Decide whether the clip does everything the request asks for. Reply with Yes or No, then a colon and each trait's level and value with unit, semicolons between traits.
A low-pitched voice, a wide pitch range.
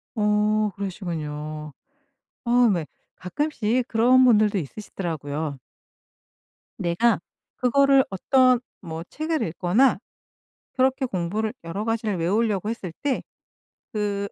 No: high, 210 Hz; wide, 5.8 semitones